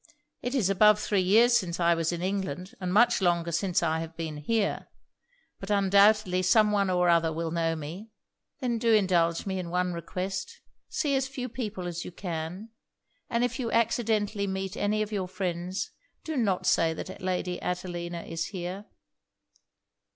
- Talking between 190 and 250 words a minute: No, average, 175 wpm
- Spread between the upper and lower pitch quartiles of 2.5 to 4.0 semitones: Yes, average, 3.6 semitones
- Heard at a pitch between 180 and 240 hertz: Yes, medium, 185 Hz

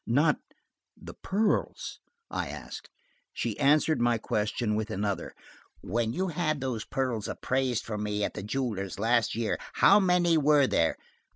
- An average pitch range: No, wide, 6.0 semitones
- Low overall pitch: Yes, low, 120 Hz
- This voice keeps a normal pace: Yes, average, 145 wpm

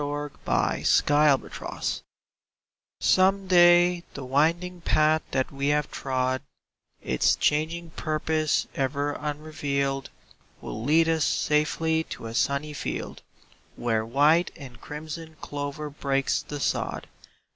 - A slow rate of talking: Yes, slow, 115 wpm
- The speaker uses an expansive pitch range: No, narrow, 2.5 semitones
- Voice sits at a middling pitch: Yes, medium, 150 Hz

